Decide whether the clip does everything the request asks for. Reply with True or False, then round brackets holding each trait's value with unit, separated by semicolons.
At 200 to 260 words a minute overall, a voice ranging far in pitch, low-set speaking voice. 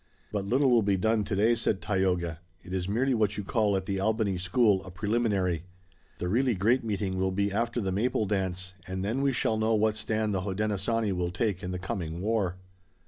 False (205 wpm; 2.9 semitones; 100 Hz)